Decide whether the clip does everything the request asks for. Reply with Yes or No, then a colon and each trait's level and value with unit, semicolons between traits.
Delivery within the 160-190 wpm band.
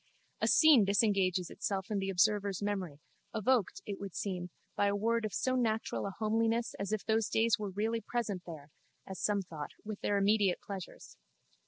Yes: average, 180 wpm